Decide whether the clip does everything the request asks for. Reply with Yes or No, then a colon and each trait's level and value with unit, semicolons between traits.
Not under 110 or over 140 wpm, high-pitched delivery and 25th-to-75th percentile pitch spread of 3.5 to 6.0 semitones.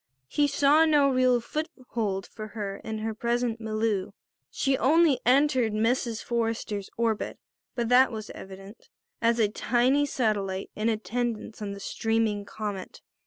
No: slow, 135 wpm; high, 225 Hz; average, 3.0 semitones